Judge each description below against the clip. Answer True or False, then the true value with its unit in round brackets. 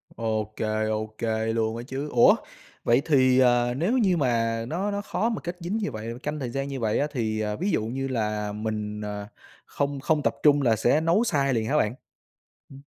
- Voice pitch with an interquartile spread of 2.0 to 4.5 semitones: False (5.1 semitones)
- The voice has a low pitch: True (120 Hz)